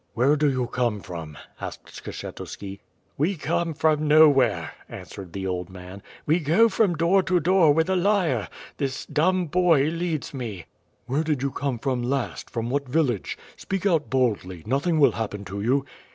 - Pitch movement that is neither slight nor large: No, wide, 6.3 semitones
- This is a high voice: No, medium, 140 Hz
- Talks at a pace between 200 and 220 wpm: No, average, 170 wpm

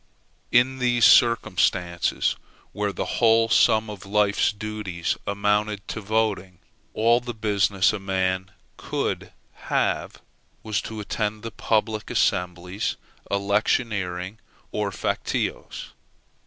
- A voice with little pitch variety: Yes, narrow, 2.3 semitones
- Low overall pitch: Yes, low, 105 Hz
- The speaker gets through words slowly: Yes, slow, 105 wpm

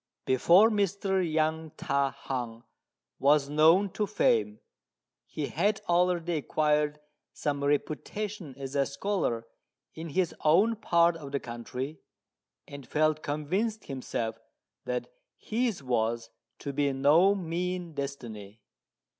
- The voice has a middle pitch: Yes, medium, 150 Hz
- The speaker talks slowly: Yes, slow, 115 wpm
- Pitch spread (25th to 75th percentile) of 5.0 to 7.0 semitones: No, average, 4.6 semitones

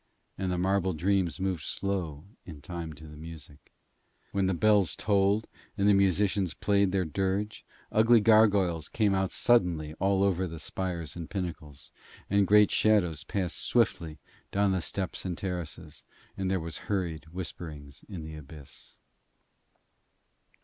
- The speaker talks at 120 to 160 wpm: Yes, average, 145 wpm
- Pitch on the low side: Yes, very low, 95 Hz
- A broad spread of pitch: No, average, 3.5 semitones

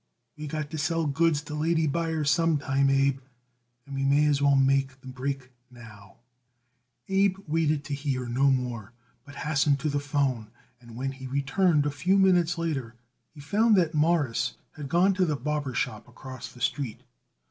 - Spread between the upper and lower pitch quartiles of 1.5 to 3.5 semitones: Yes, average, 3.1 semitones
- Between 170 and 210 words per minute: Yes, average, 180 wpm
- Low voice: No, medium, 145 Hz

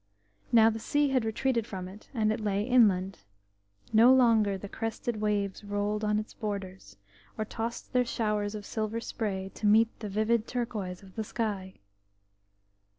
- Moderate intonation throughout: No, narrow, 2.0 semitones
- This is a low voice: No, high, 215 Hz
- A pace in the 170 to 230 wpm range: No, average, 160 wpm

